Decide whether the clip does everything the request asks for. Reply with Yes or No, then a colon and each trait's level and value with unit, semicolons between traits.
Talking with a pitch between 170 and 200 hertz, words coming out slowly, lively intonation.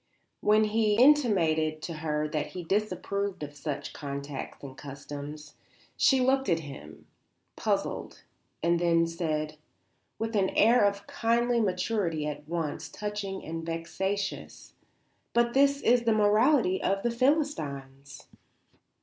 Yes: medium, 185 Hz; slow, 125 wpm; wide, 6.6 semitones